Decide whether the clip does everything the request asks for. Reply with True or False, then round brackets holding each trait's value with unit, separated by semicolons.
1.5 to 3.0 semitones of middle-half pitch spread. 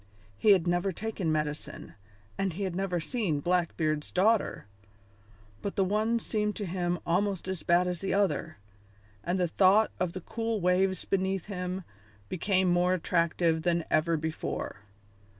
True (2.6 semitones)